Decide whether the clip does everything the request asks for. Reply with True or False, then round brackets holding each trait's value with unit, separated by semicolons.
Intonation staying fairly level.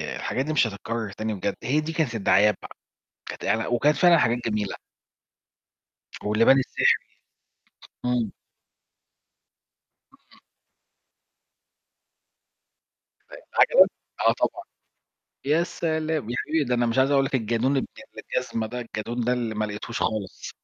False (4.1 semitones)